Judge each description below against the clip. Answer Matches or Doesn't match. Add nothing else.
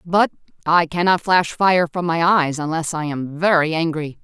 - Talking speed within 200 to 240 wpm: Doesn't match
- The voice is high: Doesn't match